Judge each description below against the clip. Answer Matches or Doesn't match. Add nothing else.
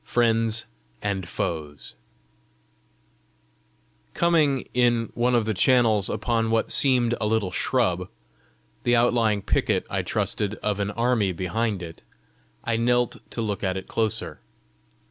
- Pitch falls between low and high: Doesn't match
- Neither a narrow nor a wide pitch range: Matches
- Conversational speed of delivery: Doesn't match